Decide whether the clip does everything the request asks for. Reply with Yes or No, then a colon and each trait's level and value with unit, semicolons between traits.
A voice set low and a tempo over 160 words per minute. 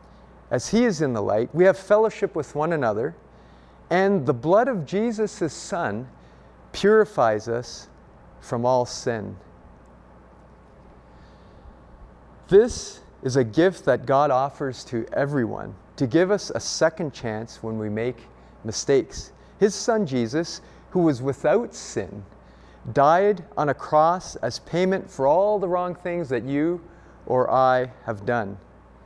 No: low, 130 Hz; average, 140 wpm